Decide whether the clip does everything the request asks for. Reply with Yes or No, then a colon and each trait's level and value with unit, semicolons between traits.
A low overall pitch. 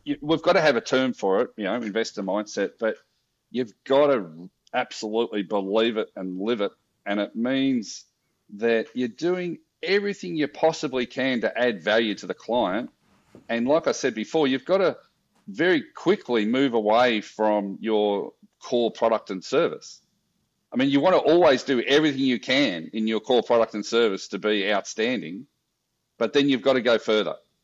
Yes: low, 125 Hz